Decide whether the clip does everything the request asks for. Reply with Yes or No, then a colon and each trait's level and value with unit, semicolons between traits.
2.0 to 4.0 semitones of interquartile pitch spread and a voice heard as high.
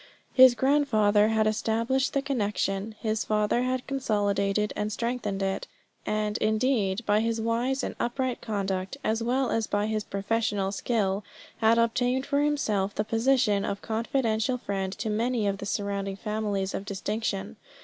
Yes: average, 3.0 semitones; high, 220 Hz